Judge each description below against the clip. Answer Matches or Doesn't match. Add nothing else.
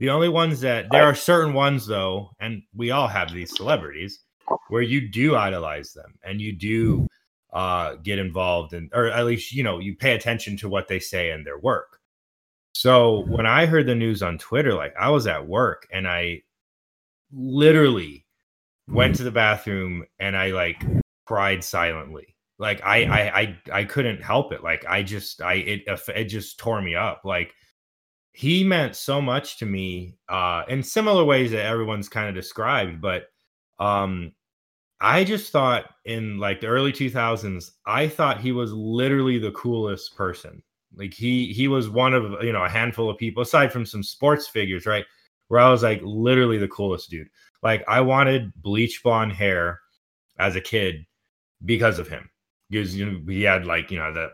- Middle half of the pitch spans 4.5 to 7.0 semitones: Matches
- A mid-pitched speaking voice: Doesn't match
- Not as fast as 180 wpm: Doesn't match